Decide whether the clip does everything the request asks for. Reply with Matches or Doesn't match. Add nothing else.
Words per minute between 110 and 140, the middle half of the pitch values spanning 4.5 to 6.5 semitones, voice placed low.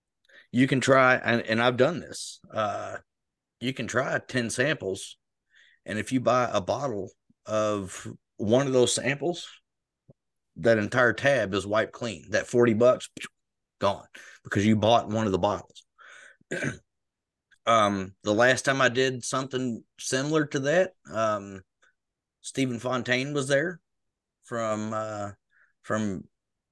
Doesn't match